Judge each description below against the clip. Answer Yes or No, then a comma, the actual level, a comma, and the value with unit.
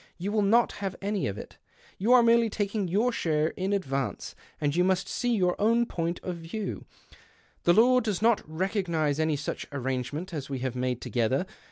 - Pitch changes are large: Yes, wide, 6.1 semitones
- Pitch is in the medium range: Yes, medium, 180 Hz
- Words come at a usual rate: Yes, average, 195 wpm